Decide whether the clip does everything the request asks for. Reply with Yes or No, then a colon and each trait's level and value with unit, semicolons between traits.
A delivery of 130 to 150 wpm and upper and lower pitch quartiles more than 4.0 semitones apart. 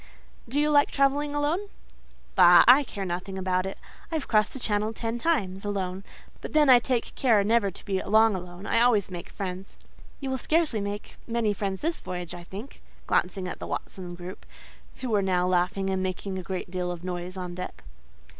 No: average, 200 wpm; average, 4.6 semitones